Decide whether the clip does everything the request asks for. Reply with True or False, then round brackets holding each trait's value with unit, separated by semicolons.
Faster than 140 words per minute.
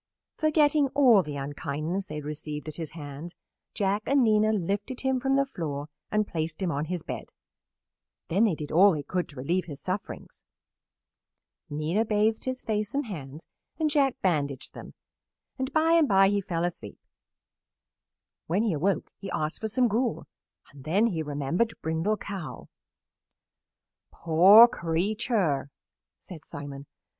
True (150 wpm)